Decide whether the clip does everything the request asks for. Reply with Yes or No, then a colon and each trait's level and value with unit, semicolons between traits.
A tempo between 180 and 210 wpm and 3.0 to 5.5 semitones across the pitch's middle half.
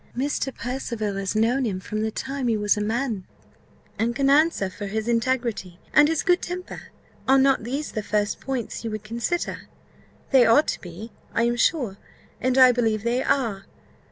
Yes: average, 185 wpm; average, 3.9 semitones